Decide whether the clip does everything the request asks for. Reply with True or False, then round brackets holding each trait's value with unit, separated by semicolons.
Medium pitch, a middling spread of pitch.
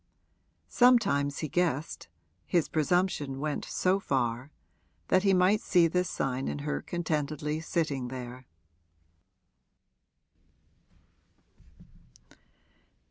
True (155 Hz; 4.7 semitones)